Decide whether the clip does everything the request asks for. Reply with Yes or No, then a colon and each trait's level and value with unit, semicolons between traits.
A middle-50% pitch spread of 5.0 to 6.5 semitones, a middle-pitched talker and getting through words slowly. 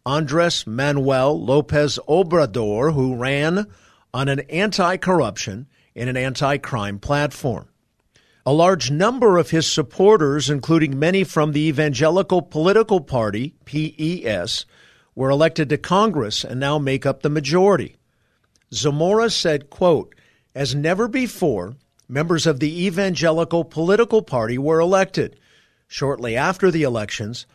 No: average, 4.5 semitones; medium, 150 Hz; slow, 120 wpm